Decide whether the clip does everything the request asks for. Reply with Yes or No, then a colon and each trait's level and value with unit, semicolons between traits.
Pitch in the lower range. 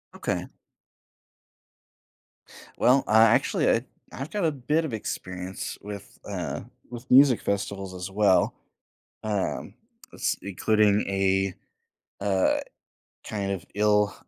Yes: low, 105 Hz